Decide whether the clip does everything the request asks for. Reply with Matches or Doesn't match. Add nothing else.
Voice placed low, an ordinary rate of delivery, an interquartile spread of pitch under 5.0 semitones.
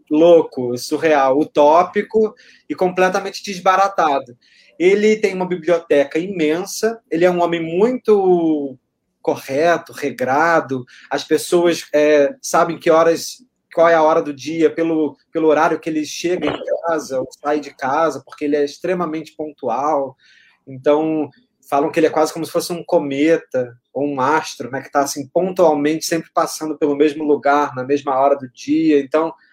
Doesn't match